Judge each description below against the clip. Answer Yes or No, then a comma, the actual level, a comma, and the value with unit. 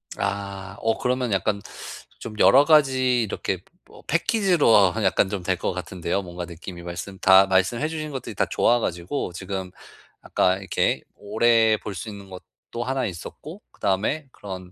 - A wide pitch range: No, average, 4.9 semitones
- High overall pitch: No, low, 100 Hz